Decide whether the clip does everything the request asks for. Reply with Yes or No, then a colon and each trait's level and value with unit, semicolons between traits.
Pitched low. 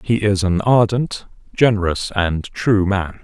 Yes: low, 100 Hz